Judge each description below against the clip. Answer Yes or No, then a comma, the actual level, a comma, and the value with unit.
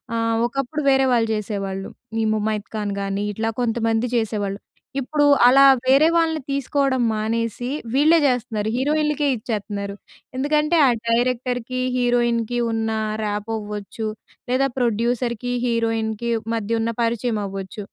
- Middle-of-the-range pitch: No, high, 230 Hz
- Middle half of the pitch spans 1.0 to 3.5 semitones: Yes, average, 2.9 semitones